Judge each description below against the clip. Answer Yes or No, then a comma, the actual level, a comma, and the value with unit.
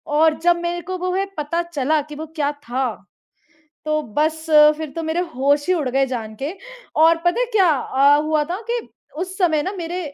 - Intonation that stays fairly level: No, average, 3.3 semitones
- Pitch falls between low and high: No, very high, 315 Hz